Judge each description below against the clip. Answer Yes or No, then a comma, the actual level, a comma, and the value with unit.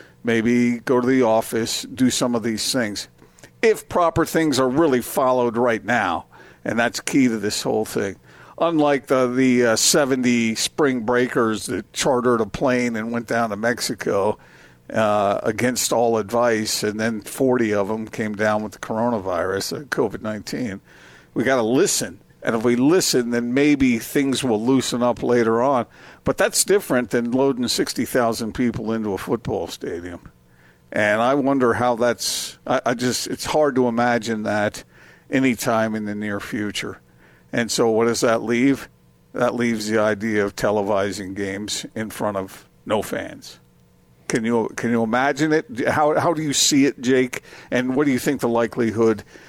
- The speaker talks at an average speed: Yes, average, 170 wpm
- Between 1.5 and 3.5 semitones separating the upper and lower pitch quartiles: Yes, average, 2.8 semitones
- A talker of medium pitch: No, low, 115 Hz